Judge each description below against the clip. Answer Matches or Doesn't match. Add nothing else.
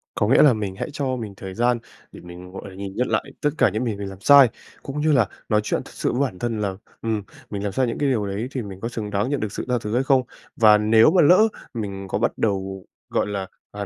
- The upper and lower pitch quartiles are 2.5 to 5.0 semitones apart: Matches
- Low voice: Matches